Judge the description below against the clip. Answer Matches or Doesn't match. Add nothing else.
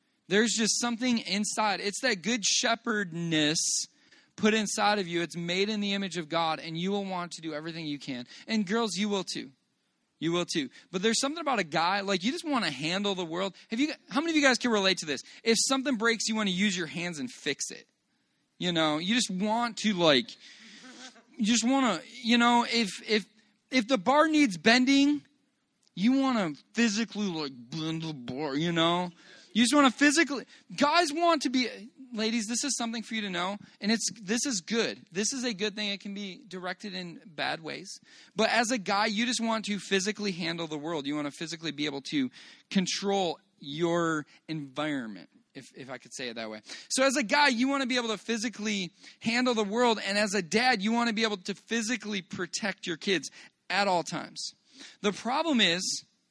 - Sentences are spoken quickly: Matches